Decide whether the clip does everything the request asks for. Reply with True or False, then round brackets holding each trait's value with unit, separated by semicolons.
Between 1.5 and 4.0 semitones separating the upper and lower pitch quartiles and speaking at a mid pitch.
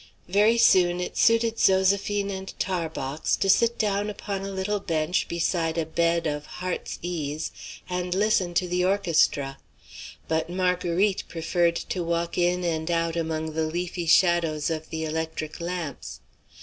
True (2.9 semitones; 175 Hz)